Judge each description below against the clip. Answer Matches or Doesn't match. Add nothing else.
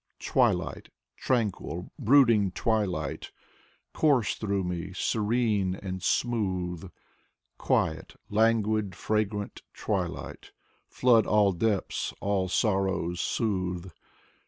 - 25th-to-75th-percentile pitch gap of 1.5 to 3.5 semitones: Matches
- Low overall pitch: Matches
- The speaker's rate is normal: Doesn't match